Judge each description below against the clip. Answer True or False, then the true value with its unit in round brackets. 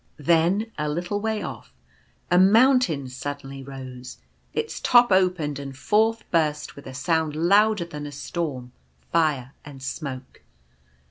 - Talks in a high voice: False (155 Hz)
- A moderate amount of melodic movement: False (5.9 semitones)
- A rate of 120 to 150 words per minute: True (140 wpm)